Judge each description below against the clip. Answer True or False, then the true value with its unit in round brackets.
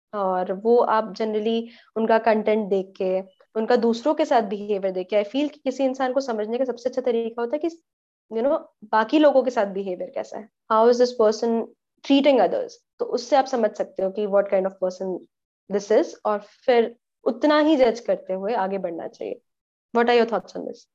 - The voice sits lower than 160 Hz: False (230 Hz)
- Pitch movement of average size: True (4.3 semitones)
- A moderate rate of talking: False (210 wpm)